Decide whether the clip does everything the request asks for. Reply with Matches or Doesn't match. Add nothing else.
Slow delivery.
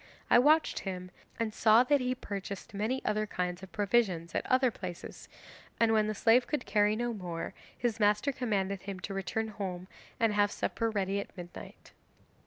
Doesn't match